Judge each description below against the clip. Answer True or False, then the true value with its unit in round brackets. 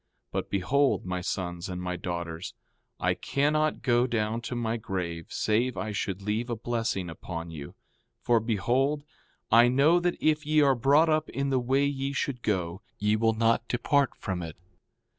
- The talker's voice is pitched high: False (115 Hz)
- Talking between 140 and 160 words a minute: False (180 wpm)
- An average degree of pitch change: False (6.6 semitones)